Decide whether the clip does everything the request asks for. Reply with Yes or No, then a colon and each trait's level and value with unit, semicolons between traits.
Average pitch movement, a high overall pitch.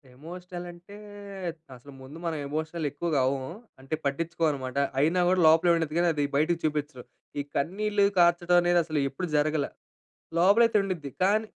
No: average, 3.3 semitones; medium, 165 Hz